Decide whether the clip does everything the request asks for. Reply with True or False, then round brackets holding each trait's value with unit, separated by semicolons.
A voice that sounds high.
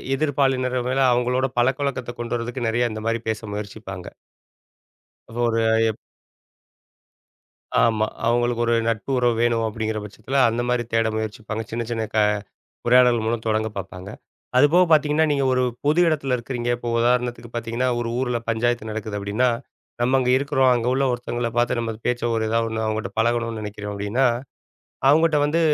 False (120 Hz)